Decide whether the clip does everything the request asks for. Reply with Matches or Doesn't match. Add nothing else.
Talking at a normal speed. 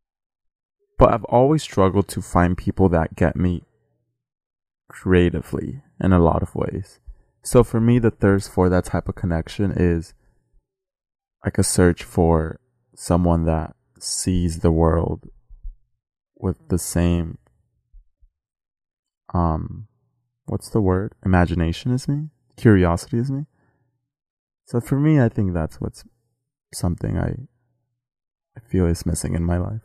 Doesn't match